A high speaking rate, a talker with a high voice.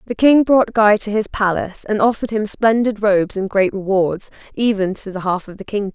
Yes: fast, 220 wpm; high, 205 Hz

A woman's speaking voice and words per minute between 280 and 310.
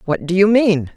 No: female; fast, 250 wpm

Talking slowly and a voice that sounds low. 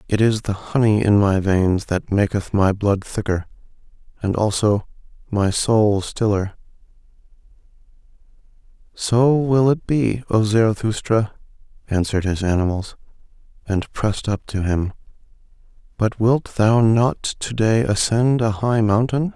Yes: slow, 125 wpm; low, 105 Hz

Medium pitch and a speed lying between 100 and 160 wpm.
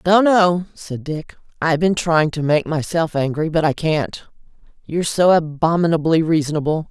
Yes: medium, 160 Hz; average, 155 wpm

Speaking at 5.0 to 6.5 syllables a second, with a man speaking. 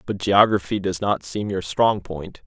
No: 4.3 syllables/s; male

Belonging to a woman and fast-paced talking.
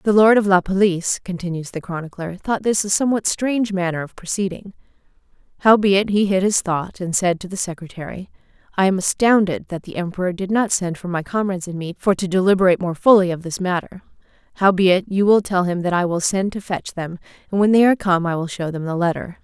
Yes: female; fast, 220 wpm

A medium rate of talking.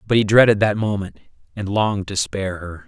No: fast, 210 wpm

